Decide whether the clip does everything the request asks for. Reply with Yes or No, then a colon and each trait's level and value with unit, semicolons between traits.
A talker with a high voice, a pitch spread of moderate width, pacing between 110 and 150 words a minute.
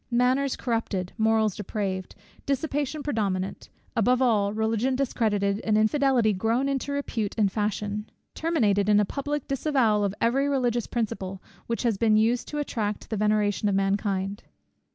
Yes: high, 220 Hz; average, 4.0 semitones; average, 145 wpm